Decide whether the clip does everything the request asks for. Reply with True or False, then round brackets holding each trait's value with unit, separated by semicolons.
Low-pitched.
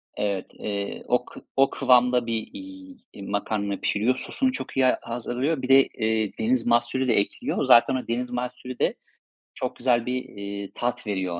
True (120 Hz)